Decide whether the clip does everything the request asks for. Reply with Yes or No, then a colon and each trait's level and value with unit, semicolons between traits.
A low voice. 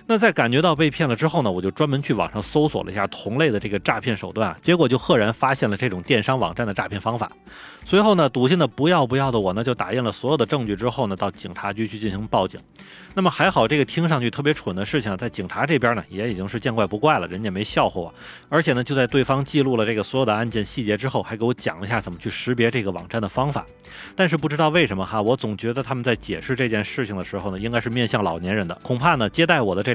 Yes: low, 120 Hz